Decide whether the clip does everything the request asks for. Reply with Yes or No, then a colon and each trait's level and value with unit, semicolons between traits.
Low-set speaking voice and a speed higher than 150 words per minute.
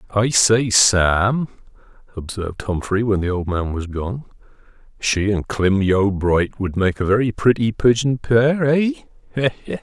No: low, 105 Hz; slow, 135 wpm